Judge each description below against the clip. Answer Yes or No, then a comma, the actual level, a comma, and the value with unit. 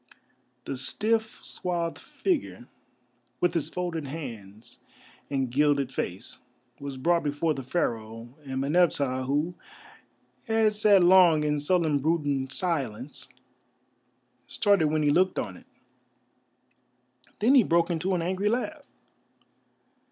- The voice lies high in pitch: No, medium, 155 Hz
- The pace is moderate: No, slow, 115 wpm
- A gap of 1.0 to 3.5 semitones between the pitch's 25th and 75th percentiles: No, average, 5.1 semitones